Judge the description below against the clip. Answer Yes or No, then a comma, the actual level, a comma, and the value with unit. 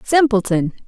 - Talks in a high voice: Yes, high, 225 Hz